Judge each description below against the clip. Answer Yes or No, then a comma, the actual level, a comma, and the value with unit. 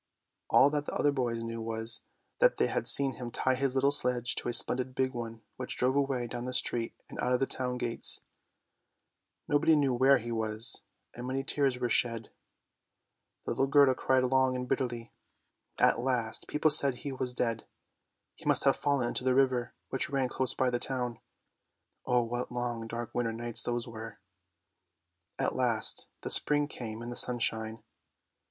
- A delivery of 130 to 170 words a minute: No, average, 180 wpm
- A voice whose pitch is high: No, low, 125 Hz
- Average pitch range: No, narrow, 2.1 semitones